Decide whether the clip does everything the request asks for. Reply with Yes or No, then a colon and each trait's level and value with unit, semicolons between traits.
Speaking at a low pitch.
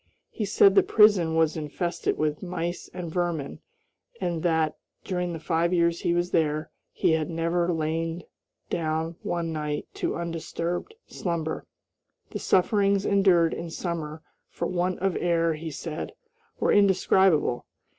No: medium, 170 Hz